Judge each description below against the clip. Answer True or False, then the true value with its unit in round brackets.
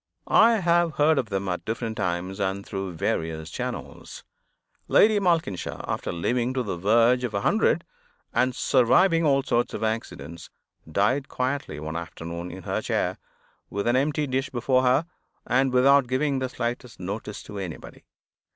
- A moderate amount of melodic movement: False (5.9 semitones)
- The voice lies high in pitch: False (120 Hz)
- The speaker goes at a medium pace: True (160 wpm)